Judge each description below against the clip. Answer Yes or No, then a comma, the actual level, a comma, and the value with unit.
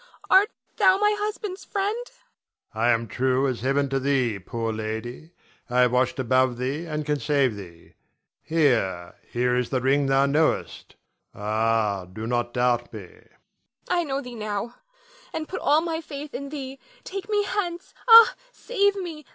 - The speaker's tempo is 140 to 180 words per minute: Yes, average, 165 wpm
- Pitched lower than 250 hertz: Yes, medium, 140 Hz